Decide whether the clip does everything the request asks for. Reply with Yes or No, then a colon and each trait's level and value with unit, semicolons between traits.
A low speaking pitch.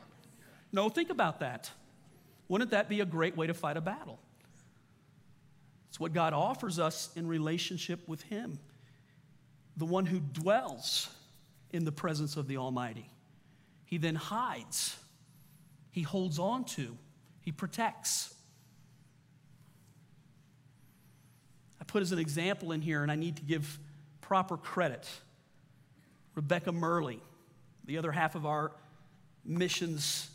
No: medium, 155 Hz